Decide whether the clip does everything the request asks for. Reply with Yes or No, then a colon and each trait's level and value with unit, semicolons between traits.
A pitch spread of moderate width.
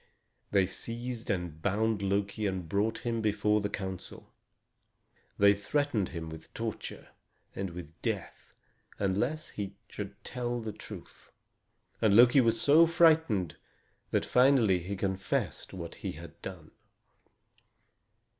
Yes: average, 3.8 semitones